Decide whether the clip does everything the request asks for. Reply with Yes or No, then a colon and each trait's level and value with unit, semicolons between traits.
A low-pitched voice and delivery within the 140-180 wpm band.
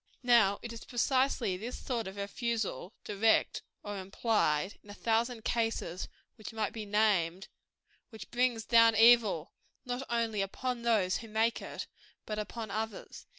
No: high, 220 Hz; average, 150 wpm